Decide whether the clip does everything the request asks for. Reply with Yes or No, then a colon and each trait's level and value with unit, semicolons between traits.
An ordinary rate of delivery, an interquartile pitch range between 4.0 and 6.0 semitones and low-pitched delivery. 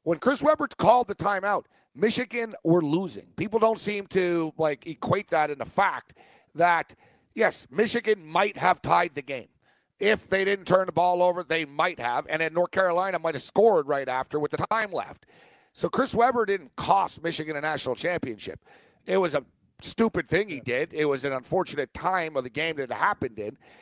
No: average, 195 wpm; average, 4.7 semitones; medium, 175 Hz